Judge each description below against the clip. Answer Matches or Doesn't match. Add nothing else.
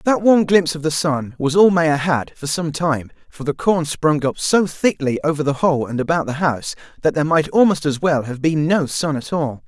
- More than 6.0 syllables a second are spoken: Doesn't match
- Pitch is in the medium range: Matches